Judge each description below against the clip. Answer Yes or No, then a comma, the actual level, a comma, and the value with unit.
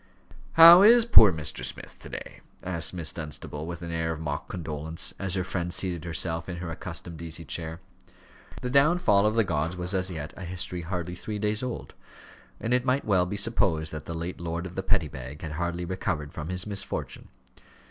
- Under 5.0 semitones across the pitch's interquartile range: Yes, average, 3.4 semitones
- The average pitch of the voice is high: No, very low, 90 Hz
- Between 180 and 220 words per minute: Yes, average, 200 wpm